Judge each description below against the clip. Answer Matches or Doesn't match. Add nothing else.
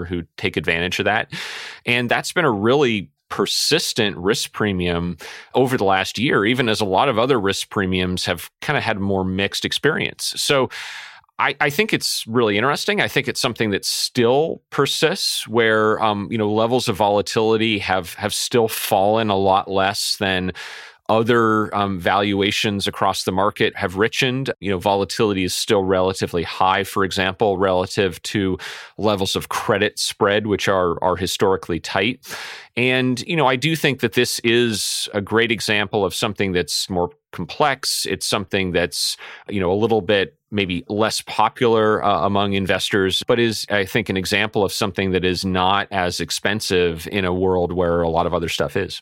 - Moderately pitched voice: Doesn't match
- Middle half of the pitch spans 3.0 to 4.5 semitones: Matches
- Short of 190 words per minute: Matches